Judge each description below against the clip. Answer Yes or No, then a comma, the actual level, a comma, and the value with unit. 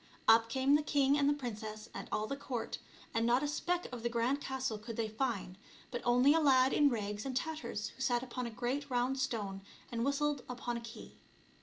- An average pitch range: Yes, average, 3.3 semitones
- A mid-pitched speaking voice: No, very high, 250 Hz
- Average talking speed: No, fast, 215 wpm